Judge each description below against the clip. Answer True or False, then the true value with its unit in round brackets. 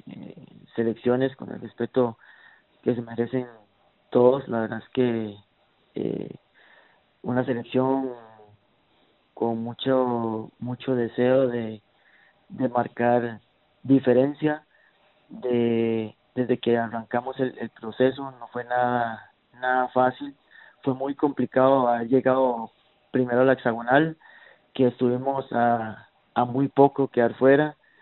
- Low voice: True (125 Hz)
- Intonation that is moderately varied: False (2.1 semitones)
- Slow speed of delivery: True (115 wpm)